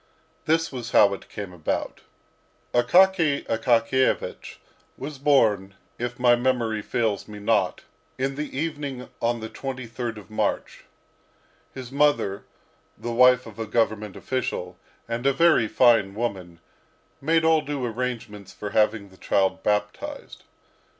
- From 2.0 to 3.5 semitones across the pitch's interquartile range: No, average, 4.2 semitones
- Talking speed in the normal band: No, slow, 130 wpm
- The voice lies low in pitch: Yes, low, 120 Hz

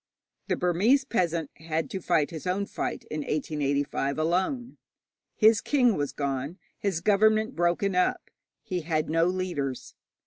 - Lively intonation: No, average, 4.5 semitones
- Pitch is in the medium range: Yes, medium, 175 Hz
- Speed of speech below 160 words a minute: Yes, average, 140 wpm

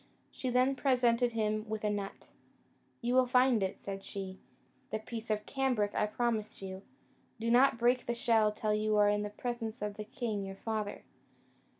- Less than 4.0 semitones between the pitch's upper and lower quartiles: Yes, average, 2.7 semitones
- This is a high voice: Yes, high, 220 Hz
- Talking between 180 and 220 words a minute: Yes, average, 190 wpm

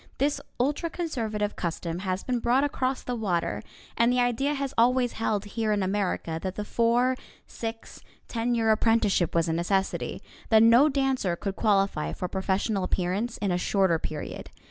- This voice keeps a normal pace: Yes, average, 170 wpm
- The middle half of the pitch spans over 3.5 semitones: Yes, average, 4.4 semitones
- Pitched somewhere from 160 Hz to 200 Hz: No, high, 220 Hz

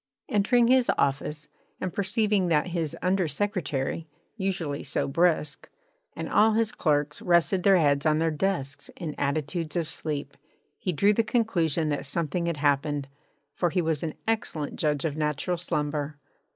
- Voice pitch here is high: No, medium, 160 Hz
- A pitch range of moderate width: Yes, average, 4.4 semitones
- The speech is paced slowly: No, average, 155 wpm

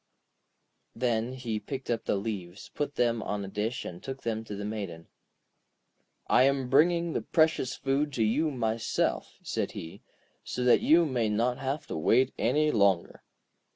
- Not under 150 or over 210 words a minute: Yes, average, 165 wpm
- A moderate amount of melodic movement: Yes, average, 4.4 semitones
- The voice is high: No, low, 120 Hz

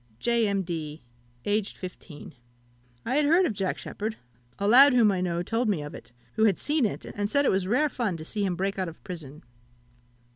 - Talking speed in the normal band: No, fast, 210 wpm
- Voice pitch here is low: No, high, 200 Hz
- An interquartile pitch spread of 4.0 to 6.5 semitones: Yes, average, 4.8 semitones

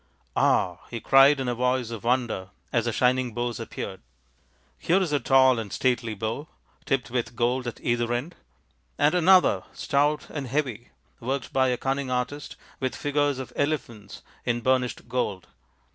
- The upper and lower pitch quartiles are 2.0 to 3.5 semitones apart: Yes, average, 2.8 semitones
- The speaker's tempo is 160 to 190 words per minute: Yes, average, 170 wpm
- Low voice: Yes, low, 125 Hz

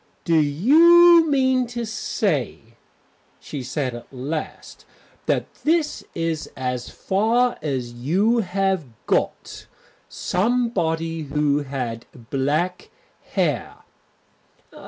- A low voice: No, medium, 165 Hz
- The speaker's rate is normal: No, slow, 95 wpm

